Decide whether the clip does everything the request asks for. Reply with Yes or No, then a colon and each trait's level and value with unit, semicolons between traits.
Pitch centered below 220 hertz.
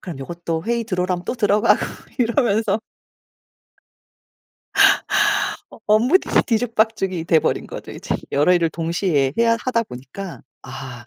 Yes: high, 190 Hz